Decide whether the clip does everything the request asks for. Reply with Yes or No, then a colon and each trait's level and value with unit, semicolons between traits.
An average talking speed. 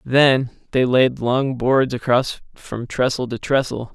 Yes: average, 150 wpm